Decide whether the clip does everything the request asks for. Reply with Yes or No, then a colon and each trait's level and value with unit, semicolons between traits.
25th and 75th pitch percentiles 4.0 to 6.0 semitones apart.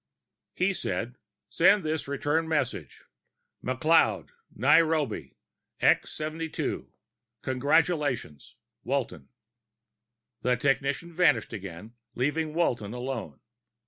Yes: average, 4.8 semitones